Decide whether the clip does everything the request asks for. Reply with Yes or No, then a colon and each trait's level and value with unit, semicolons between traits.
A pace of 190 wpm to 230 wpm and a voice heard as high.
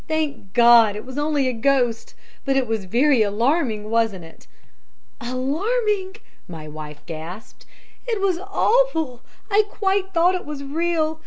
No: average, 145 wpm; very high, 270 Hz